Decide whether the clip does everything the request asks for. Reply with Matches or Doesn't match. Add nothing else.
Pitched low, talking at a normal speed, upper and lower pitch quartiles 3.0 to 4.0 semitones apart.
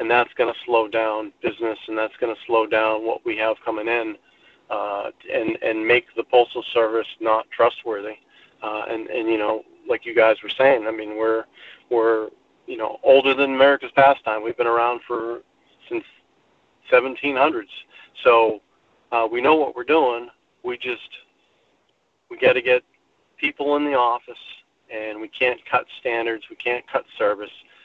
Matches